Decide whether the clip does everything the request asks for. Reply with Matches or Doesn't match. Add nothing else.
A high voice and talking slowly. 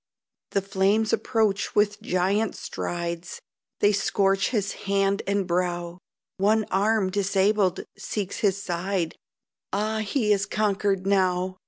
Matches